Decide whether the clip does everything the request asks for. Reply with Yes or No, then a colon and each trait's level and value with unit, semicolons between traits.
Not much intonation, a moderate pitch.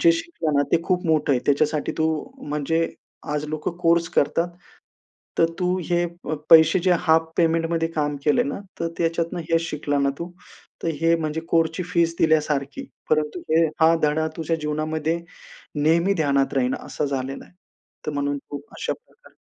Yes: narrow, 2.1 semitones; medium, 160 Hz